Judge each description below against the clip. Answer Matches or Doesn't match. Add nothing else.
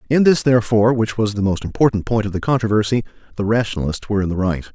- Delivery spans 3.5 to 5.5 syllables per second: Doesn't match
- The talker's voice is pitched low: Matches